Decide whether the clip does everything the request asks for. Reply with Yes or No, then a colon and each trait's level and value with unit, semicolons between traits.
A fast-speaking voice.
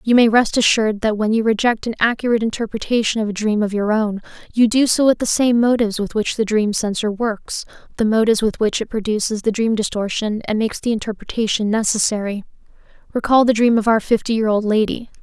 Yes: fast, 210 wpm